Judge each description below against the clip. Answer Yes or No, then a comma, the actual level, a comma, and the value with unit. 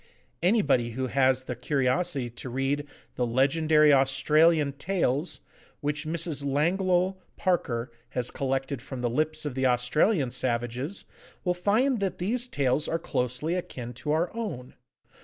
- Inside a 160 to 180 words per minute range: No, average, 140 wpm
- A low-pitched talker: No, medium, 145 Hz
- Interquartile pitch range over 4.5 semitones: Yes, average, 4.9 semitones